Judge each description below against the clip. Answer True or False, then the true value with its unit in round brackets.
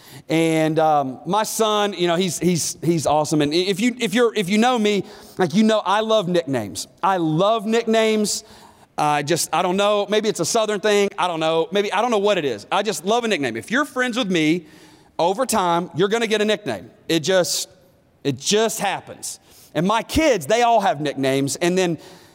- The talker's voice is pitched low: False (185 Hz)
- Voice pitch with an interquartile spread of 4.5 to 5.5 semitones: True (5.1 semitones)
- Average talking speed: False (235 wpm)